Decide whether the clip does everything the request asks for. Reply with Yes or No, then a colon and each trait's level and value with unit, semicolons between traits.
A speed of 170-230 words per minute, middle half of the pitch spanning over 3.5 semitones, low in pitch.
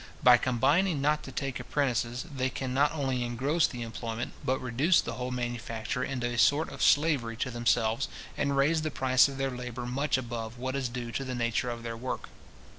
No: average, 200 wpm; narrow, 2.5 semitones; low, 125 Hz